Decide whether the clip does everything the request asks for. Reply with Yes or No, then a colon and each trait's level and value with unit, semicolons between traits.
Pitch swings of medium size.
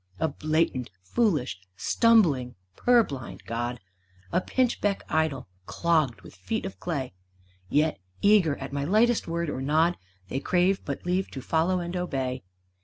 No: wide, 5.7 semitones